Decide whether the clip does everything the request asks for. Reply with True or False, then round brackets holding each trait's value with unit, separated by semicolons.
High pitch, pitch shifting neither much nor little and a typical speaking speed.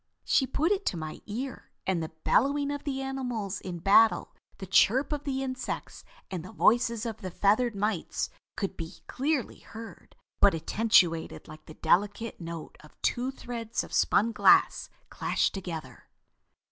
False (220 Hz; 5.9 semitones; 160 wpm)